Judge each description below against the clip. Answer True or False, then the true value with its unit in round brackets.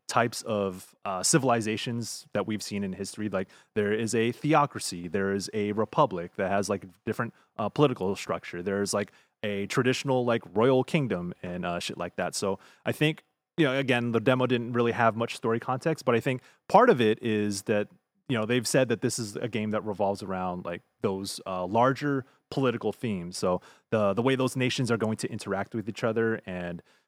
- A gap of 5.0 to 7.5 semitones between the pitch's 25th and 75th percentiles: False (4.1 semitones)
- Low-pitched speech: True (115 Hz)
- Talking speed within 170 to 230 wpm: True (200 wpm)